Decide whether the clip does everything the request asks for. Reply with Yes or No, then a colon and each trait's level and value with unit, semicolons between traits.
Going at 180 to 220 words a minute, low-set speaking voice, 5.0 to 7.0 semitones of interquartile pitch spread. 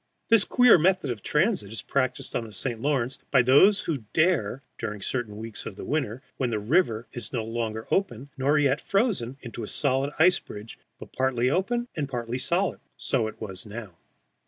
Yes: average, 185 wpm; low, 130 Hz; wide, 5.4 semitones